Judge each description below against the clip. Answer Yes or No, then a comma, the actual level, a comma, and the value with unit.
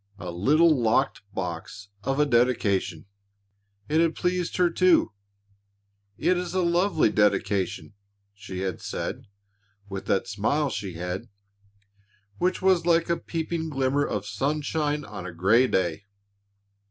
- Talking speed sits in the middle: No, slow, 130 wpm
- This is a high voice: No, low, 130 Hz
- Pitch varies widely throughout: Yes, wide, 8.9 semitones